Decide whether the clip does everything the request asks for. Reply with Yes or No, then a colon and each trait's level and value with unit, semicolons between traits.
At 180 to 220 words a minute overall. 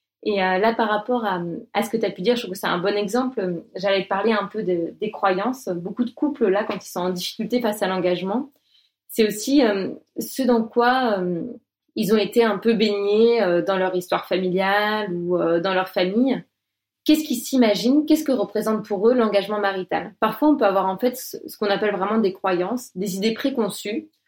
Yes: average, 215 wpm